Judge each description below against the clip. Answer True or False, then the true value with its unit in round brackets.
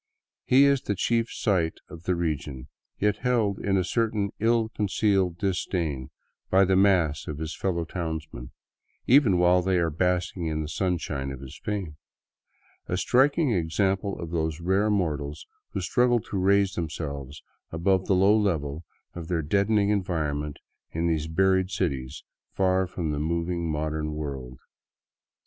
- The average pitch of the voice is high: False (90 Hz)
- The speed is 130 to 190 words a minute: True (155 wpm)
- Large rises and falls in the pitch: False (4.1 semitones)